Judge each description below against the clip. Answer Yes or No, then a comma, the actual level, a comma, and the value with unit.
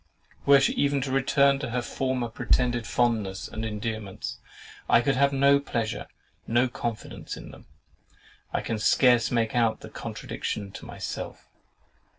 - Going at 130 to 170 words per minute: Yes, average, 150 wpm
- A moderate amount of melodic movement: Yes, average, 3.3 semitones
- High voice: No, low, 120 Hz